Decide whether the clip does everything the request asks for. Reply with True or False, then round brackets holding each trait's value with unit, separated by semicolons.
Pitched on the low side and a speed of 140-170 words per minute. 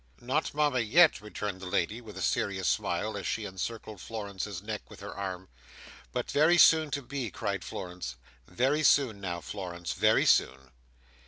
True (105 Hz; 165 wpm)